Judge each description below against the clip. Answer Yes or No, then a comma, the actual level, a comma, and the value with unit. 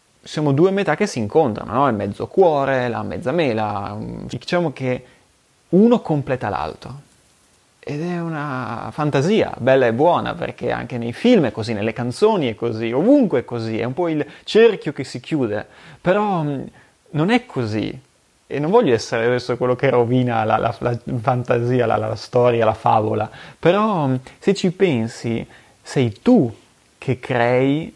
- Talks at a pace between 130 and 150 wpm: No, average, 160 wpm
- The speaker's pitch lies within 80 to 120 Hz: No, low, 130 Hz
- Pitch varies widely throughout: Yes, wide, 5.8 semitones